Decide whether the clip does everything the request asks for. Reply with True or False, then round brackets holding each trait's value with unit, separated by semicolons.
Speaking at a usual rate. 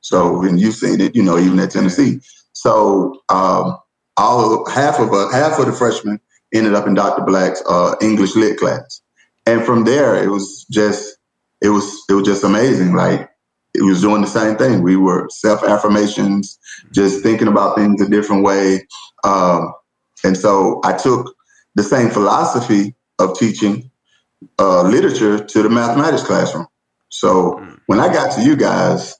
True (165 wpm)